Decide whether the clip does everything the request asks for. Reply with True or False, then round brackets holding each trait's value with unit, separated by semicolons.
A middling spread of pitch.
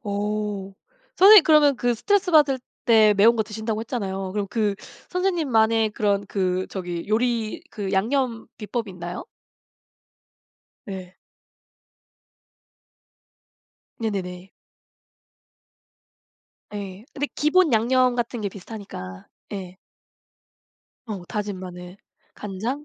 True (4.0 semitones)